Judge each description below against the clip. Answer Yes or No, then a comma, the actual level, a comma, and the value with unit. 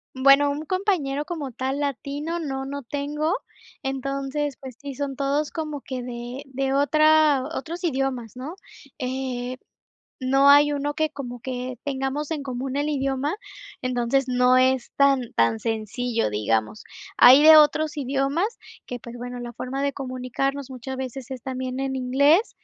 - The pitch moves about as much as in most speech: No, narrow, 2.3 semitones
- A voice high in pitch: Yes, very high, 270 Hz